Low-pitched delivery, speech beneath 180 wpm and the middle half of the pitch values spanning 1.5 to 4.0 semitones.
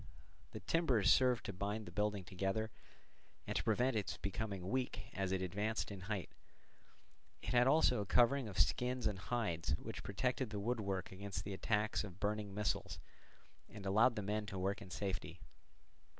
Yes: low, 105 Hz; average, 170 wpm; average, 3.0 semitones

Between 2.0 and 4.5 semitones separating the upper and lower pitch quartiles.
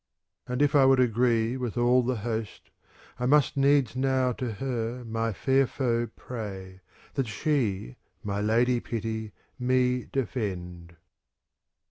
Yes: average, 2.8 semitones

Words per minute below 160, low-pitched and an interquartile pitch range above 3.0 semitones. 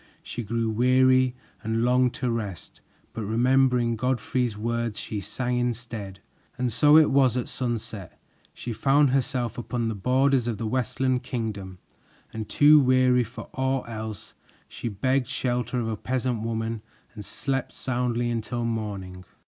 No: average, 150 wpm; low, 120 Hz; narrow, 2.4 semitones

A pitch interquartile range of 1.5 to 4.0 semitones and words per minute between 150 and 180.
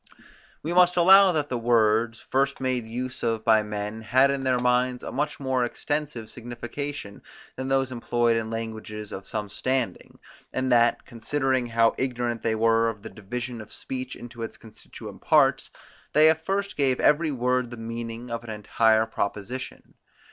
Yes: average, 2.7 semitones; average, 170 wpm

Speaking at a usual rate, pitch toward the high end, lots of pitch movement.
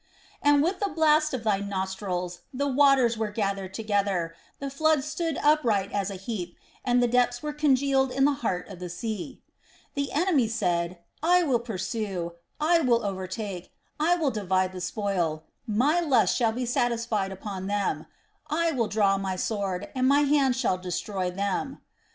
Yes: average, 165 wpm; high, 225 Hz; wide, 6.4 semitones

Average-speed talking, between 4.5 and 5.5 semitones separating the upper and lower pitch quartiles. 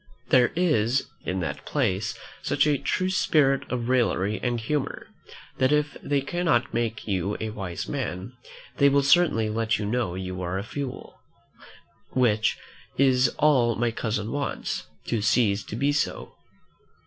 Yes: average, 150 wpm; average, 4.8 semitones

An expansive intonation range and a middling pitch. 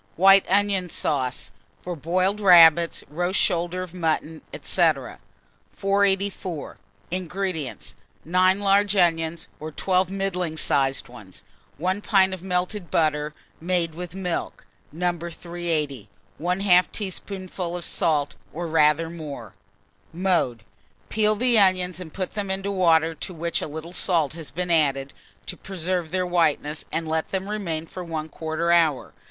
No: average, 2.9 semitones; medium, 175 Hz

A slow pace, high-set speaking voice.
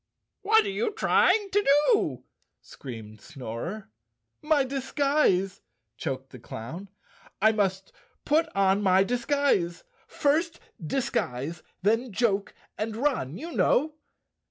Yes: slow, 110 wpm; high, 215 Hz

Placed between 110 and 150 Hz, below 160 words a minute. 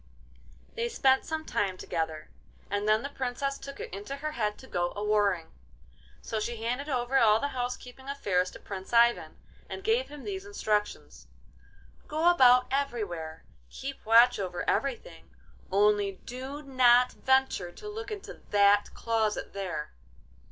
No: high, 240 Hz; average, 150 wpm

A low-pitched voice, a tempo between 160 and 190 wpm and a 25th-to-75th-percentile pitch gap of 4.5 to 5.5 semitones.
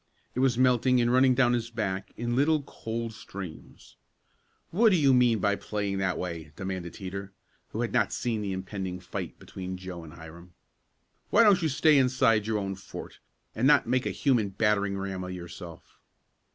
Yes: low, 105 Hz; average, 180 wpm; average, 5.2 semitones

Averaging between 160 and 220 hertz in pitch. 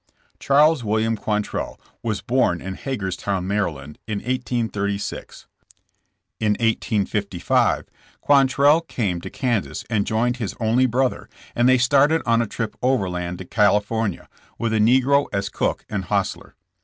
No: low, 110 Hz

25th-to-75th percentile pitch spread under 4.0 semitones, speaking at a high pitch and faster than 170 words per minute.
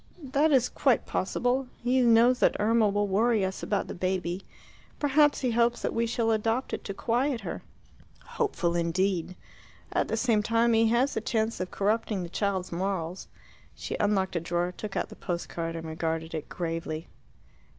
No: average, 4.8 semitones; high, 210 Hz; average, 180 wpm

